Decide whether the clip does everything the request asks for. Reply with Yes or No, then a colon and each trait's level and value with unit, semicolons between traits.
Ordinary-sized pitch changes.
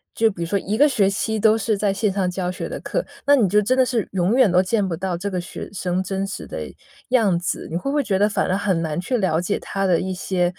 Yes: average, 3.1 semitones